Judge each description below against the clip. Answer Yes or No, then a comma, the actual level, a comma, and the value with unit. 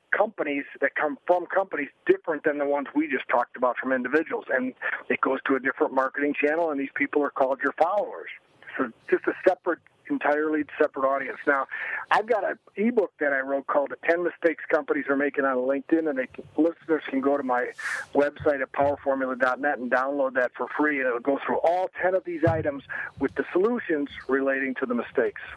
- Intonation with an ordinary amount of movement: Yes, average, 3.6 semitones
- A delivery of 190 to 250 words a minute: Yes, average, 200 wpm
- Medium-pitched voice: Yes, medium, 145 Hz